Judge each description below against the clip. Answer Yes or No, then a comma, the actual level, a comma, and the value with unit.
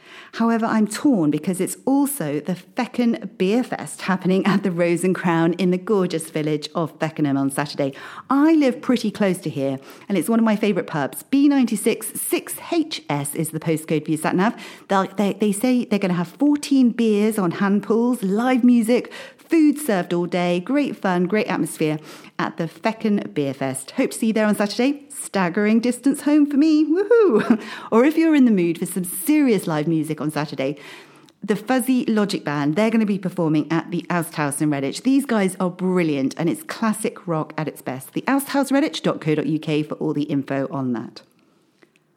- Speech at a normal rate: Yes, average, 190 wpm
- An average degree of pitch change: No, wide, 7.3 semitones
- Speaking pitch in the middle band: No, high, 195 Hz